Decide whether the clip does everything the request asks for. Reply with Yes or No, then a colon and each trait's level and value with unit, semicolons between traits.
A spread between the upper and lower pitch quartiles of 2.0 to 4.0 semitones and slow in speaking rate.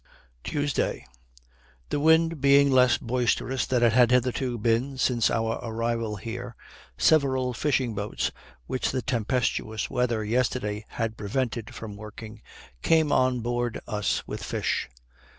Yes: narrow, 2.5 semitones; slow, 130 wpm